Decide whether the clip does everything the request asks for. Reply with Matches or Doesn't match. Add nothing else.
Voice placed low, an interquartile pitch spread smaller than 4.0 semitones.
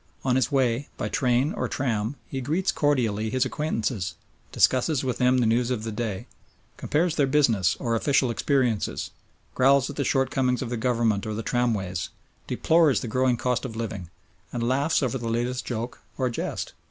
Matches